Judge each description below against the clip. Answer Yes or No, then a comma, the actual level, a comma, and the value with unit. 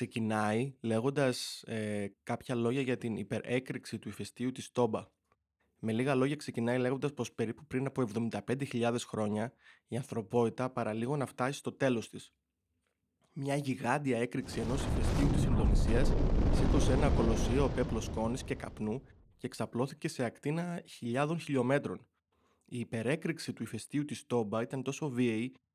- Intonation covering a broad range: No, average, 2.9 semitones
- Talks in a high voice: No, low, 120 Hz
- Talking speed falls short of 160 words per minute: Yes, average, 140 wpm